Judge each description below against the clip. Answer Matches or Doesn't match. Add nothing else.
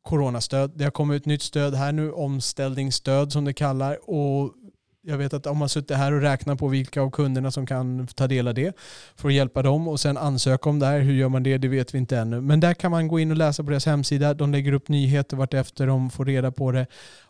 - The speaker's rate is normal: Doesn't match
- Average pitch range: Doesn't match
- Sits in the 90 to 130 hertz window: Doesn't match